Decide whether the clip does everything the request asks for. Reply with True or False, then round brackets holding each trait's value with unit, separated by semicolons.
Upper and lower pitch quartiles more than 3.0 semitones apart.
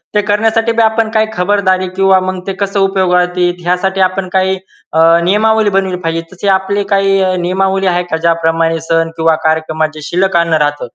False (2.6 semitones)